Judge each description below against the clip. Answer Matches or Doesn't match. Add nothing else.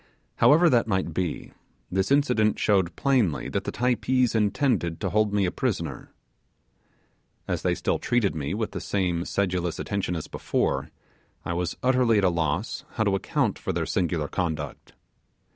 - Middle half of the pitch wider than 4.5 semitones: Matches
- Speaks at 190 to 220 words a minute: Doesn't match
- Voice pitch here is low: Matches